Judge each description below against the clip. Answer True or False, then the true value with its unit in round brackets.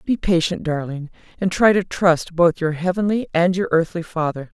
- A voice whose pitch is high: False (175 Hz)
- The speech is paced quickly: False (185 wpm)